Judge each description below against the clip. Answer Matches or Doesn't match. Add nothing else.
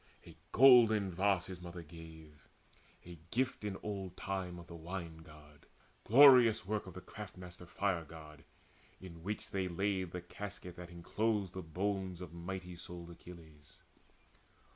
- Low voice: Matches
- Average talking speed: Matches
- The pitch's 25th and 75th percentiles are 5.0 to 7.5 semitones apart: Doesn't match